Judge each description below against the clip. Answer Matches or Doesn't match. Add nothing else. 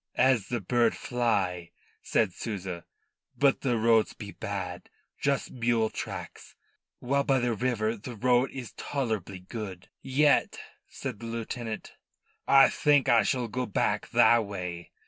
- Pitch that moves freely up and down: Doesn't match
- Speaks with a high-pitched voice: Doesn't match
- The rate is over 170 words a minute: Doesn't match